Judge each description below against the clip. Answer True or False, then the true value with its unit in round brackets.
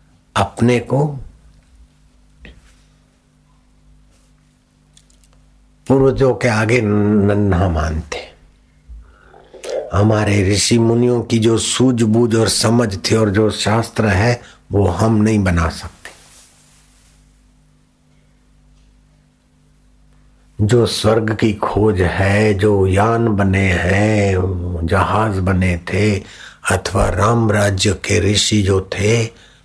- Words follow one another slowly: True (85 wpm)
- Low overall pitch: True (105 Hz)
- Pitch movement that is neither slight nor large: True (3.6 semitones)